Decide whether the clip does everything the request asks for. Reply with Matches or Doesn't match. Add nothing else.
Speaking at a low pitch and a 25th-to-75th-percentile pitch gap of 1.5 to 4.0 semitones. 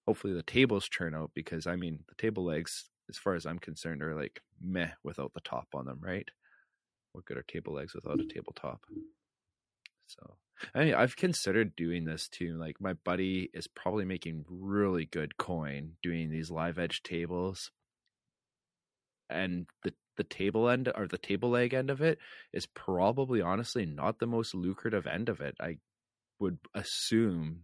Doesn't match